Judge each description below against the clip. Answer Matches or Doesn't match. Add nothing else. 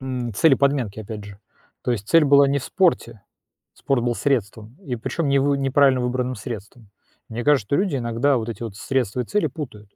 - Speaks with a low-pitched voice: Matches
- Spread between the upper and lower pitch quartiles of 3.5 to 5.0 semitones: Matches